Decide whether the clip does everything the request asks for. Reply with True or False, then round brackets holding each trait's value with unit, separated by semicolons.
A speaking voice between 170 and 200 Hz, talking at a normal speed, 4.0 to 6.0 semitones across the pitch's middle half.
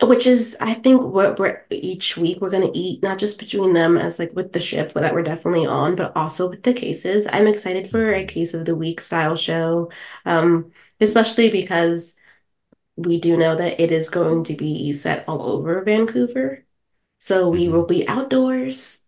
True (185 Hz; 190 wpm; 4.8 semitones)